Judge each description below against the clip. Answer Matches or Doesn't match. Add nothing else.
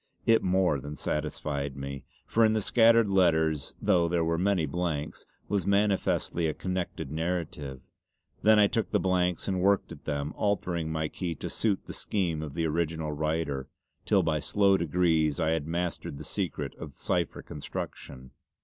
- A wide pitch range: Doesn't match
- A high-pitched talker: Doesn't match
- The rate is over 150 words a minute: Matches